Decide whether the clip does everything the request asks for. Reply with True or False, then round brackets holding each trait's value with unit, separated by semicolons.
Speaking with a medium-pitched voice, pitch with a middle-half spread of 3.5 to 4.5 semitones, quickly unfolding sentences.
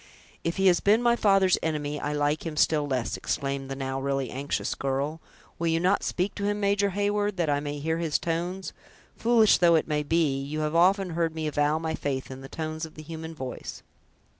True (160 Hz; 4.0 semitones; 215 wpm)